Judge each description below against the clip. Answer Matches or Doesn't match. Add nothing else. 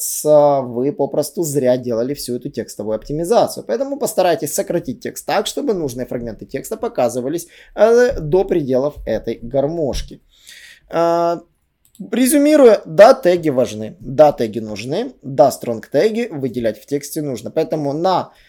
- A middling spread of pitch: Doesn't match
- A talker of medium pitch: Matches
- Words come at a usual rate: Matches